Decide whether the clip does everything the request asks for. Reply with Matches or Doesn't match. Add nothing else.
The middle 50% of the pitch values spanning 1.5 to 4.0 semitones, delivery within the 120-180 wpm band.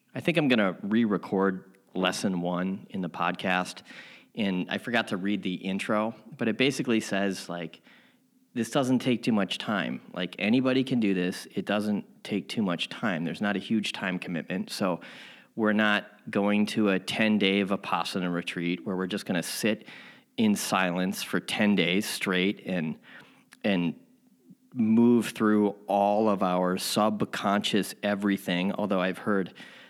Matches